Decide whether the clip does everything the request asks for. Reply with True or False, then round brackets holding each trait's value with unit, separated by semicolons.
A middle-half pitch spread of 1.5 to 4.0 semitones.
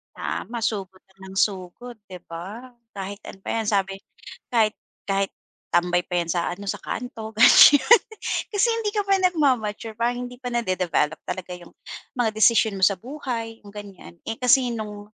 False (4.4 semitones)